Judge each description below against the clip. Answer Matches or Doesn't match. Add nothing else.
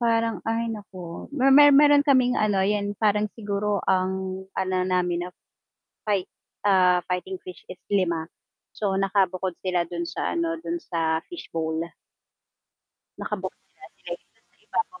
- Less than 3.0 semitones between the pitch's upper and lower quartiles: Doesn't match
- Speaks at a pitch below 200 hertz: Matches